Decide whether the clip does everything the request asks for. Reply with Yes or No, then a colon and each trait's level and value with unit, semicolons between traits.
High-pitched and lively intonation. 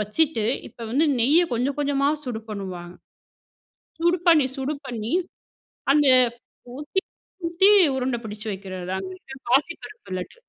Yes: very high, 250 Hz; wide, 6.0 semitones